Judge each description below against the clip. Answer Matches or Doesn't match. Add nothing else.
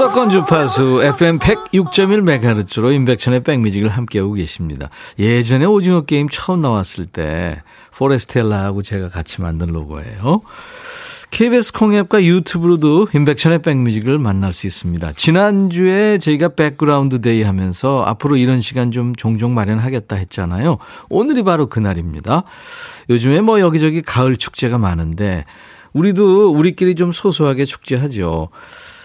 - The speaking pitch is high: Doesn't match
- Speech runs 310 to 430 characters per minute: Matches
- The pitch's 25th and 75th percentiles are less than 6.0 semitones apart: Doesn't match